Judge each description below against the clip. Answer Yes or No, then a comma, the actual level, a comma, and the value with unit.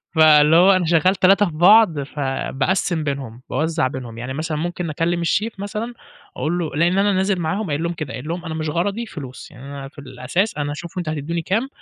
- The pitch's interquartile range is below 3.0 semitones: No, average, 4.2 semitones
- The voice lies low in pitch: No, medium, 165 Hz